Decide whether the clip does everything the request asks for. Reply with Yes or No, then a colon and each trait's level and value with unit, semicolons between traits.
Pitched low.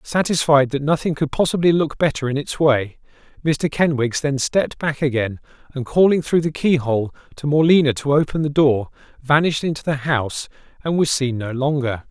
No: medium, 145 Hz